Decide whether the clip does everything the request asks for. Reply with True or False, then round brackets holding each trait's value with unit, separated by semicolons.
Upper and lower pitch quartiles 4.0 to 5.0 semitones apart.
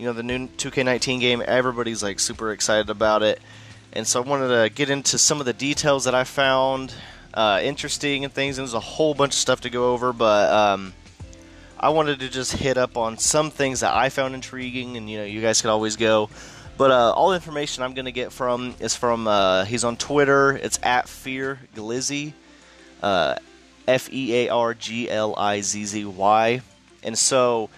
False (3.6 semitones)